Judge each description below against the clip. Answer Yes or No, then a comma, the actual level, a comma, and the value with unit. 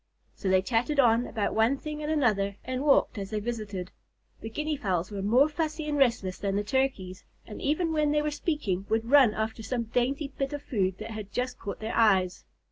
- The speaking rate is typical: No, fast, 210 wpm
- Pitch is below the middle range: No, high, 230 Hz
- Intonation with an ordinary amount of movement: No, wide, 5.9 semitones